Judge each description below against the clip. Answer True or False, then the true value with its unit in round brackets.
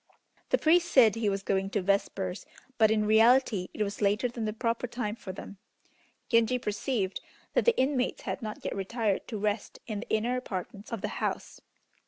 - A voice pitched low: False (215 Hz)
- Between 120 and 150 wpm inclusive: False (190 wpm)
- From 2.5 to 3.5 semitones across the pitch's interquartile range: True (3.2 semitones)